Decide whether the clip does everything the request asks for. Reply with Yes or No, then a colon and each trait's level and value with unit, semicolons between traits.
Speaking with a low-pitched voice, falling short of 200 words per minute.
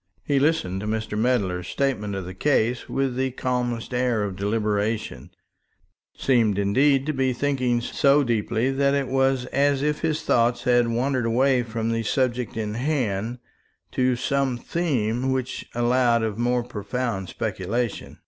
Yes: low, 120 Hz; average, 150 wpm